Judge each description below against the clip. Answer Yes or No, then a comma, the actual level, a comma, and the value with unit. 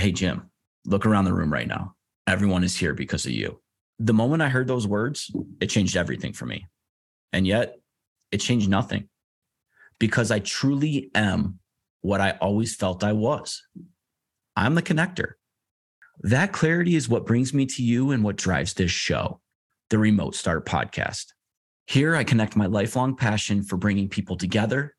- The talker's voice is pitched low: Yes, low, 105 Hz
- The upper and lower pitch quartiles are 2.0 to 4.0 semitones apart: No, average, 4.8 semitones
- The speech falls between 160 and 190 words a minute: Yes, average, 170 wpm